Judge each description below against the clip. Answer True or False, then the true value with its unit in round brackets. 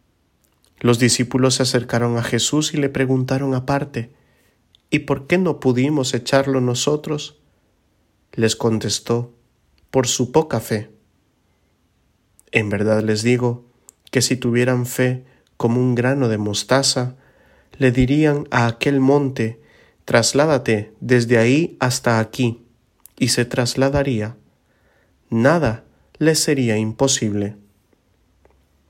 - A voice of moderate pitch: False (125 Hz)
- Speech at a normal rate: False (110 wpm)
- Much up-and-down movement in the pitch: False (3.2 semitones)